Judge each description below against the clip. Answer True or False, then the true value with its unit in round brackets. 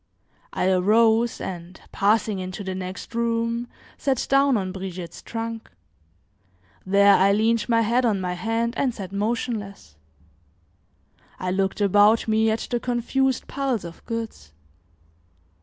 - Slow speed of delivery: True (130 wpm)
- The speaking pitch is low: False (220 Hz)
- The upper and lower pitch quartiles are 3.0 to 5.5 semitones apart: True (3.4 semitones)